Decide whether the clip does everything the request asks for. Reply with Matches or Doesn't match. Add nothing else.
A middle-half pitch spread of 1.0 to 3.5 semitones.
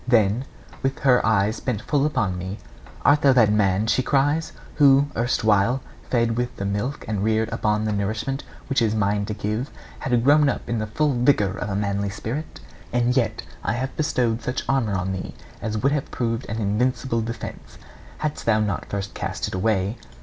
Doesn't match